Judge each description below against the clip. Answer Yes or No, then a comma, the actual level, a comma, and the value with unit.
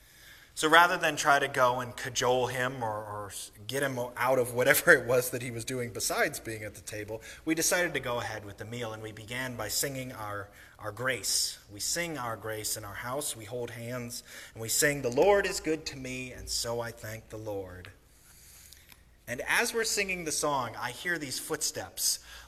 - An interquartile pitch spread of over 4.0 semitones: Yes, average, 4.4 semitones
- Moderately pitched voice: No, low, 120 Hz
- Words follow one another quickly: Yes, fast, 210 wpm